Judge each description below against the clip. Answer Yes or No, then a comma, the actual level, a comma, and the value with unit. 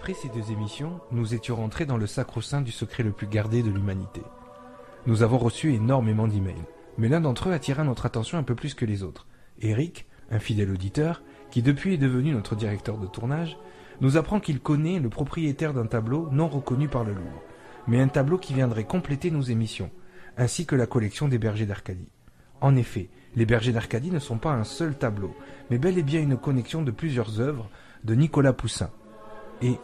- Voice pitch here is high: No, low, 120 Hz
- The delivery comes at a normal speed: Yes, average, 200 wpm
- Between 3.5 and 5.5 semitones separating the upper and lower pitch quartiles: Yes, average, 4.6 semitones